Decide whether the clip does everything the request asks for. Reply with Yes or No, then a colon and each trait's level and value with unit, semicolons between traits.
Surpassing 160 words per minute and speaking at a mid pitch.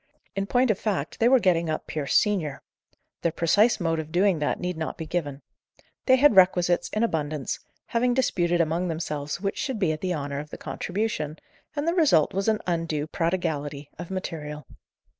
Yes: average, 185 wpm; medium, 175 Hz